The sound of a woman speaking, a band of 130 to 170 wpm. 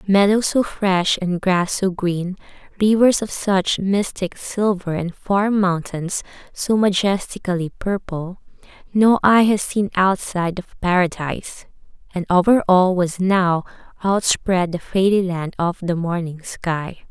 Yes: female; slow, 135 wpm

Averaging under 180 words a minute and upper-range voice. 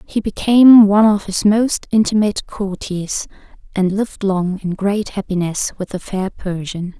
Yes: average, 155 wpm; high, 200 Hz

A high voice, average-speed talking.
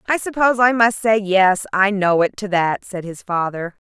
No: high, 200 Hz; fast, 215 wpm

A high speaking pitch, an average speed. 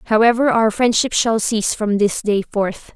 Yes: high, 220 Hz; average, 180 wpm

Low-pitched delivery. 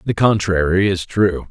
Yes: very low, 95 Hz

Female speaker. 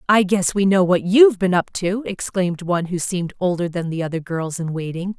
Yes: female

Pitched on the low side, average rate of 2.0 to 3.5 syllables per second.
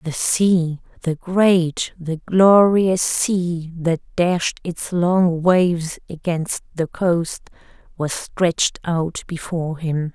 No: medium, 170 Hz; 3.0 syllables/s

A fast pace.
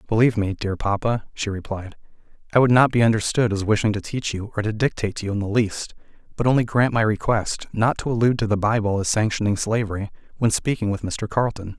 Yes: fast, 220 wpm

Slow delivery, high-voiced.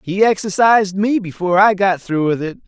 No: average, 200 wpm; high, 195 Hz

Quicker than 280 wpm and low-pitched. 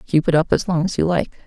No: fast, 325 wpm; medium, 165 Hz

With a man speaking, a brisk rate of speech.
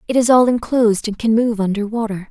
No: female; fast, 235 wpm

